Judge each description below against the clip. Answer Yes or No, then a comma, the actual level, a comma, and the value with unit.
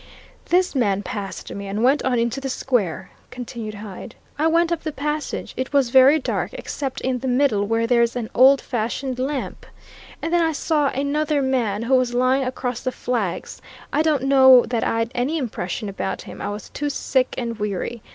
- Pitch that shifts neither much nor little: Yes, average, 3.4 semitones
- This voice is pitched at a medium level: No, very high, 255 Hz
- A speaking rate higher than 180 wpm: Yes, average, 190 wpm